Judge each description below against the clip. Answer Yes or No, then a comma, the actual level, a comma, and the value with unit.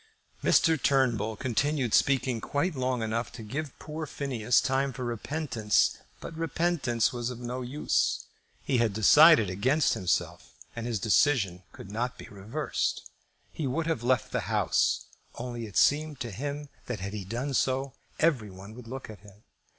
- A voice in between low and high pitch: No, low, 125 Hz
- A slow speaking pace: No, average, 165 wpm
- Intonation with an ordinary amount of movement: Yes, average, 4.4 semitones